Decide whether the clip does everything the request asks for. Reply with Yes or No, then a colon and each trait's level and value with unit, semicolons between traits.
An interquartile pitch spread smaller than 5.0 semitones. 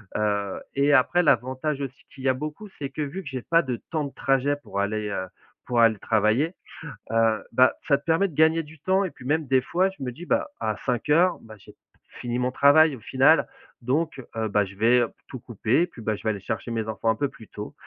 No: wide, 5.5 semitones